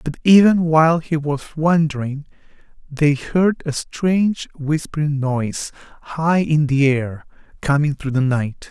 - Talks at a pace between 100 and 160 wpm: Yes, average, 140 wpm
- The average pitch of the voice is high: No, medium, 150 Hz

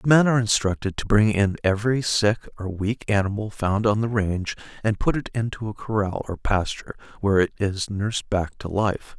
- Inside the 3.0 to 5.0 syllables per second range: No, 5.5 syllables/s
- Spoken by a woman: No, male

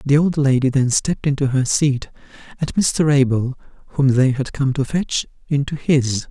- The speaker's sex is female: No, male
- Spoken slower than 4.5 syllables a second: Yes, 4.1 syllables/s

